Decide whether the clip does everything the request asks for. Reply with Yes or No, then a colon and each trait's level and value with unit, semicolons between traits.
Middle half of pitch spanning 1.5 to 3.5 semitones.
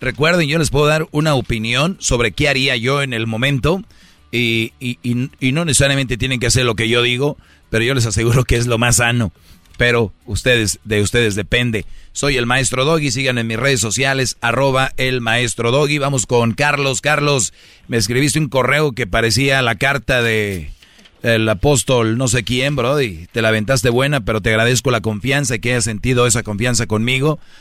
Yes: average, 3.1 semitones